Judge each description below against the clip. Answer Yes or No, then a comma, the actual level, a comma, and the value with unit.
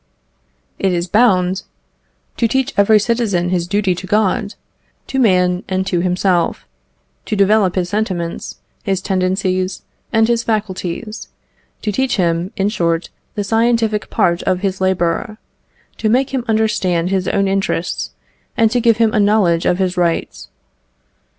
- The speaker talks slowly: No, average, 145 wpm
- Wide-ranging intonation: No, average, 3.2 semitones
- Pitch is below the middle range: No, high, 195 Hz